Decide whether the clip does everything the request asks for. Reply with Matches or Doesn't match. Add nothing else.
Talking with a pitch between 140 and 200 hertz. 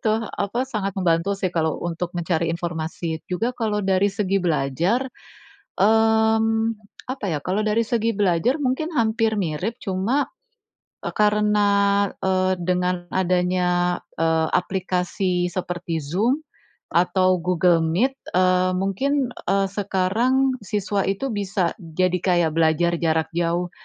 Matches